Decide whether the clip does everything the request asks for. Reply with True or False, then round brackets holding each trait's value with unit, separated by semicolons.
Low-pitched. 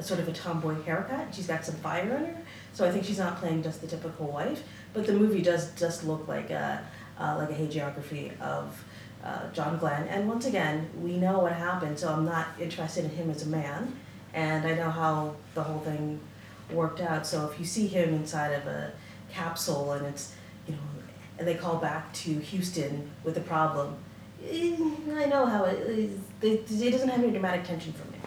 False (165 Hz)